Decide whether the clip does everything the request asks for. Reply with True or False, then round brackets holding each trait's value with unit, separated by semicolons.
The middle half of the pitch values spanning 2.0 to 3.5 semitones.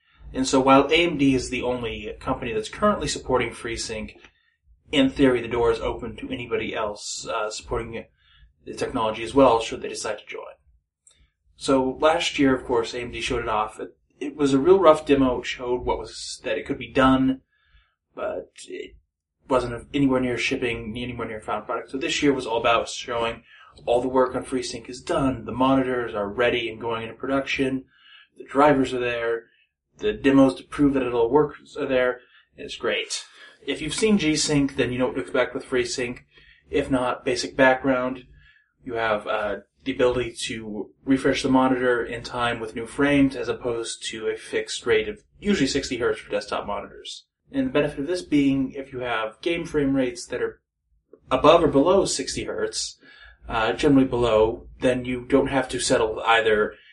True (3.2 semitones)